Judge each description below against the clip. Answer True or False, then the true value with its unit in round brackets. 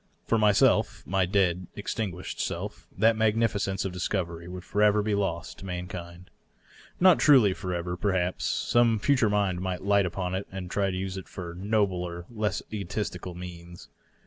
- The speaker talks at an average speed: True (160 wpm)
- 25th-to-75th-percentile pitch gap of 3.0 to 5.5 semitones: False (2.6 semitones)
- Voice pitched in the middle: False (95 Hz)